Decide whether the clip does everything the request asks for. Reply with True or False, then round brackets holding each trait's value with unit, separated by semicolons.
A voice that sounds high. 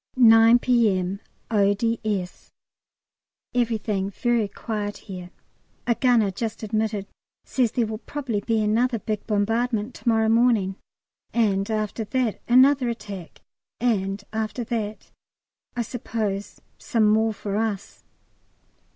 True (220 Hz)